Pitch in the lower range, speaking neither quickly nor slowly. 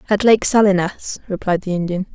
No: high, 195 Hz; average, 170 wpm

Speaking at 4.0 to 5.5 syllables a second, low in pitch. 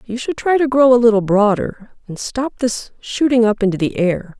No: 4.9 syllables/s; high, 230 Hz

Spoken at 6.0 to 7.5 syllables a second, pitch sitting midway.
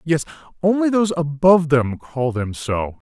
No: 4.8 syllables/s; medium, 155 Hz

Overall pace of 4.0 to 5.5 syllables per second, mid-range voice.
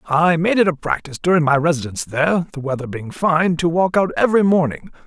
No: 6.2 syllables/s; medium, 160 Hz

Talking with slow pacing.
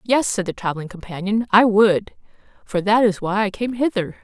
No: average, 200 wpm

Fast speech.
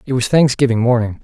No: average, 195 wpm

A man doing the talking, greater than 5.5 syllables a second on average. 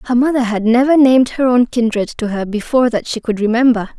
No: female; 5.9 syllables/s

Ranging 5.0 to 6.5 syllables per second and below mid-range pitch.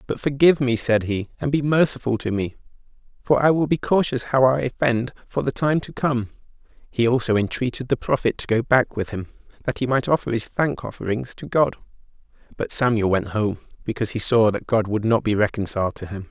Yes: 5.8 syllables/s; low, 120 Hz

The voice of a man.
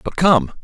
Yes: male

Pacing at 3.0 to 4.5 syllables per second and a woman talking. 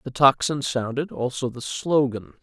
No: 4.4 syllables/s; male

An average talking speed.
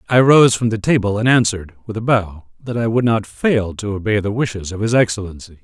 No: fast, 235 wpm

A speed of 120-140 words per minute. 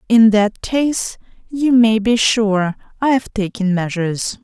Yes: slow, 135 wpm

